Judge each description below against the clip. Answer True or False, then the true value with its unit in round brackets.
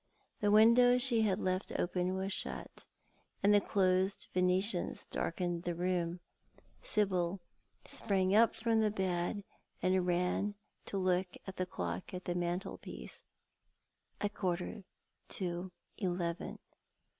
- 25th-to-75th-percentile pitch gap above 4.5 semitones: False (2.4 semitones)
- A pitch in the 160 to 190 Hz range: True (185 Hz)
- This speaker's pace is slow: True (120 wpm)